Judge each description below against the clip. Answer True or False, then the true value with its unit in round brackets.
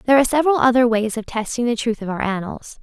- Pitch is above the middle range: True (235 Hz)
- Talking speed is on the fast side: True (255 wpm)